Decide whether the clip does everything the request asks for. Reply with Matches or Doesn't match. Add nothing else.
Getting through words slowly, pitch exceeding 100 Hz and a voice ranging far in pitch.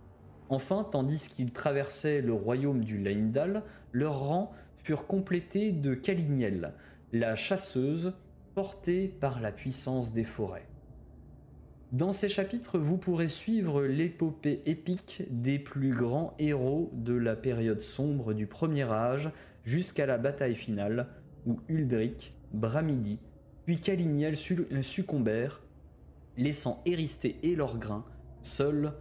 Matches